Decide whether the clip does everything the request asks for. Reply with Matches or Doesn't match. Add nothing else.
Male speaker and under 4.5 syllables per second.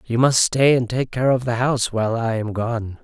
Doesn't match